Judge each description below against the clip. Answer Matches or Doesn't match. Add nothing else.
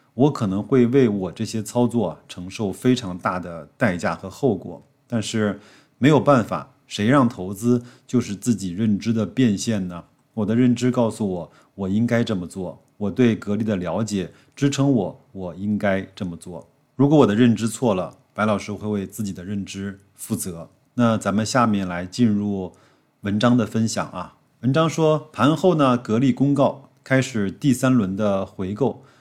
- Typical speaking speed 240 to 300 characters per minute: Matches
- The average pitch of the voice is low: Matches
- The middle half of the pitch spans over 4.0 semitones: Matches